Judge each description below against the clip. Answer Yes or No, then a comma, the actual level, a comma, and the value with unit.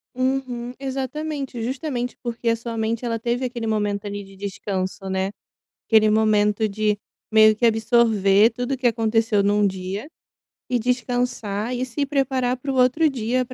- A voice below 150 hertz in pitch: No, high, 230 Hz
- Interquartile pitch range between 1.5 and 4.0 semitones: Yes, average, 3.1 semitones